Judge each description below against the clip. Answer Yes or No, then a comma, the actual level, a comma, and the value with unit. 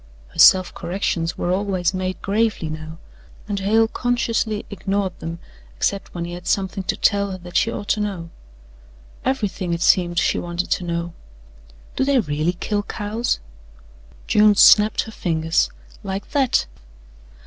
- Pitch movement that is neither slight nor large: Yes, average, 3.3 semitones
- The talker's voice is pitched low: No, high, 190 Hz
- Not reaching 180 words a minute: Yes, average, 150 wpm